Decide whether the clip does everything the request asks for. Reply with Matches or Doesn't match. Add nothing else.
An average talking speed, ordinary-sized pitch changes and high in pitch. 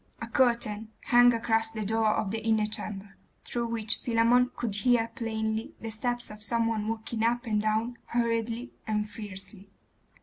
Doesn't match